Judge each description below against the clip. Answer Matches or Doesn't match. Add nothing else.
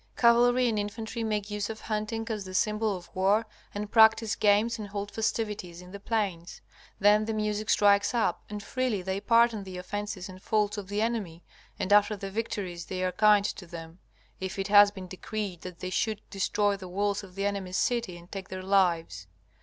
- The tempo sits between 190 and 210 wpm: Matches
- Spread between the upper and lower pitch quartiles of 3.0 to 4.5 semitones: Doesn't match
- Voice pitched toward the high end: Matches